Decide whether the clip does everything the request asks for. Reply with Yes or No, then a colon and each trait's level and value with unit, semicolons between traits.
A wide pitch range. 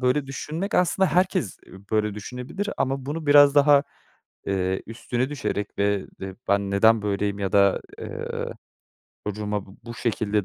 Yes: wide, 6.0 semitones